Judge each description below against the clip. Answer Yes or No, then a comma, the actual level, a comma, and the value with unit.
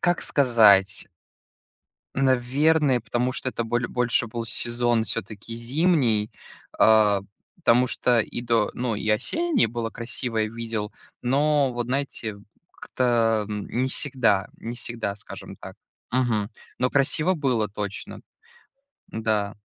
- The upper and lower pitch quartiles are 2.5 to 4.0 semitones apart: Yes, average, 2.8 semitones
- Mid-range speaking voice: No, low, 120 Hz